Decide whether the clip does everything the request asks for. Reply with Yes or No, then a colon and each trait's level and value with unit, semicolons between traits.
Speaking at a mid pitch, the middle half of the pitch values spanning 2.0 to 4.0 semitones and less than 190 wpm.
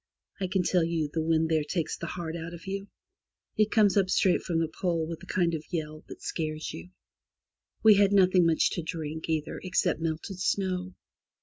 No: medium, 170 Hz; average, 2.7 semitones; average, 200 wpm